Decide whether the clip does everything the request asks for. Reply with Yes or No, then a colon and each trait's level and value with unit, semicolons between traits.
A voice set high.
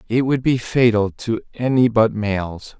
No: low, 115 Hz